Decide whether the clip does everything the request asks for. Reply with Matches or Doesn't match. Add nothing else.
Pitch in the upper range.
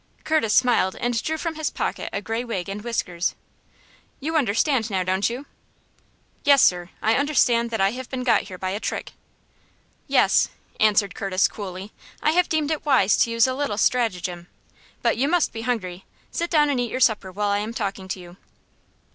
Matches